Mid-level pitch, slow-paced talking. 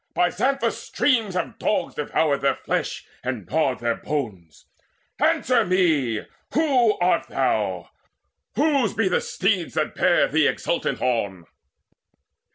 Yes: medium, 175 Hz; slow, 125 wpm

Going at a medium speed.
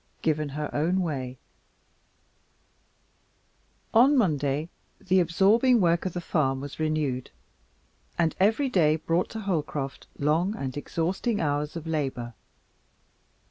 No: slow, 115 wpm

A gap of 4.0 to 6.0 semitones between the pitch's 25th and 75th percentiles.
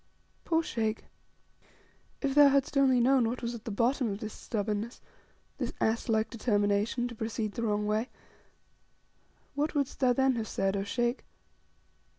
No: average, 3.4 semitones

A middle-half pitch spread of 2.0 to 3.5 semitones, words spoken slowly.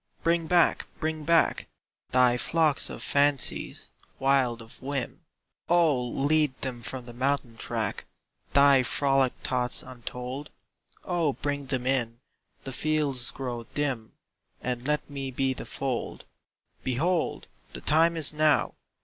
Yes: average, 3.2 semitones; slow, 130 wpm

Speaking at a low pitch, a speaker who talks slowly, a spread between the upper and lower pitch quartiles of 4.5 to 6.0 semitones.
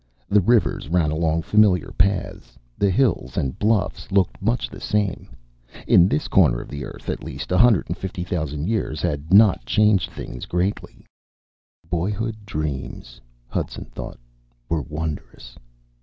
Yes: very low, 90 Hz; slow, 130 wpm; average, 5.0 semitones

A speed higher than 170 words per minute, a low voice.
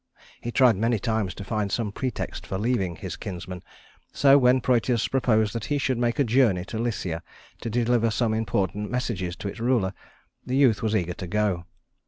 Yes: average, 190 wpm; low, 110 Hz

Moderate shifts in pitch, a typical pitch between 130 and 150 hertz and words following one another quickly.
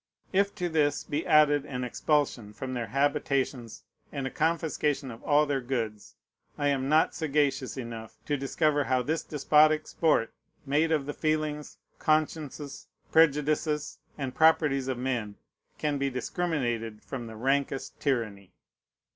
No: average, 3.0 semitones; medium, 140 Hz; average, 140 wpm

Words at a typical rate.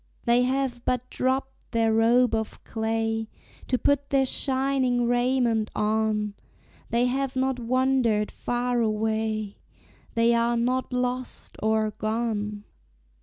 No: slow, 120 wpm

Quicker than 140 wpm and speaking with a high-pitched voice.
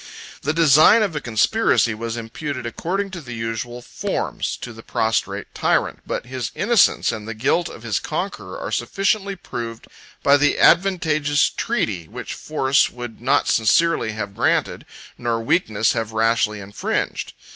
No: average, 155 wpm; low, 120 Hz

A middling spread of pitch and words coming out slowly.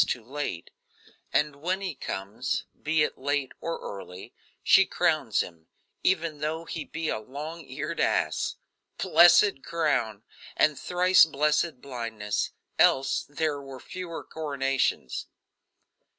Yes: average, 4.7 semitones; slow, 120 wpm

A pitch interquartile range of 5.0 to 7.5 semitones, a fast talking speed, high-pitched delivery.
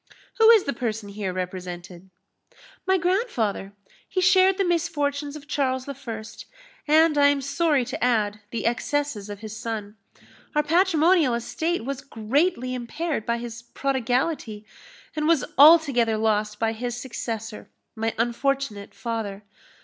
No: wide, 5.6 semitones; slow, 135 wpm; very high, 250 Hz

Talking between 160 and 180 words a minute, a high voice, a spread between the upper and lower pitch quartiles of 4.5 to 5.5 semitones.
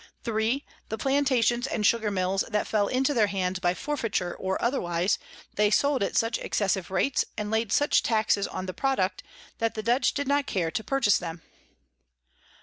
Yes: average, 175 wpm; high, 220 Hz; average, 4.9 semitones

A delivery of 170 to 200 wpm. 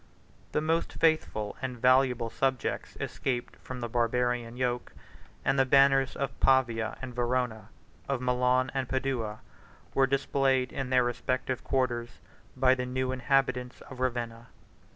No: slow, 135 wpm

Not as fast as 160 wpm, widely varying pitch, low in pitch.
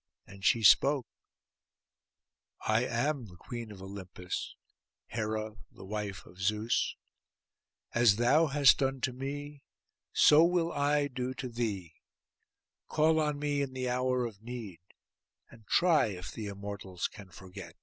Yes: average, 140 wpm; wide, 5.7 semitones; low, 120 Hz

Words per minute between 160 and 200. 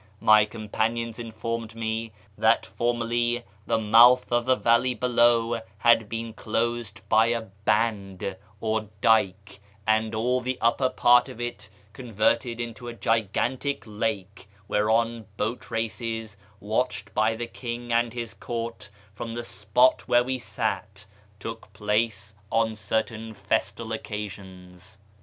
No: slow, 135 wpm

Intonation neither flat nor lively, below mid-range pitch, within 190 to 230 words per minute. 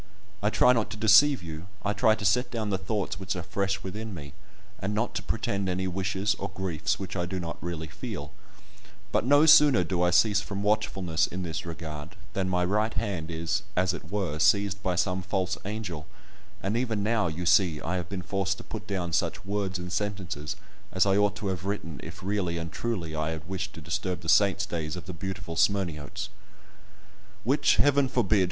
Yes: average, 3.0 semitones; very low, 95 Hz; average, 200 wpm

